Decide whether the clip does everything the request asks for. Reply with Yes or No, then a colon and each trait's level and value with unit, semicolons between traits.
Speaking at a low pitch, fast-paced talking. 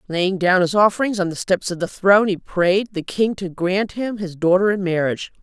No: high, 190 Hz; fast, 230 wpm